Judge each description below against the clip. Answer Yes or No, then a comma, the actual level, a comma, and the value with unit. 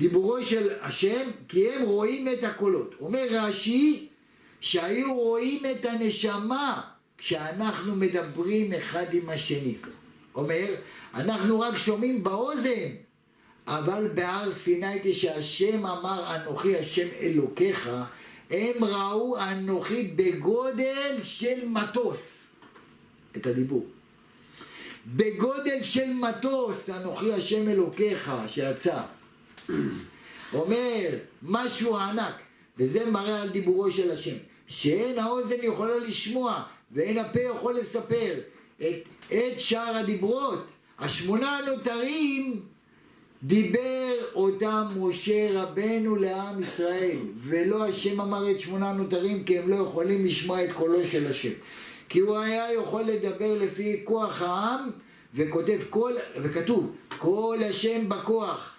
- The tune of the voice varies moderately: Yes, average, 4.4 semitones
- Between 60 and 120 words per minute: Yes, average, 105 wpm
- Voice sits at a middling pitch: No, high, 210 Hz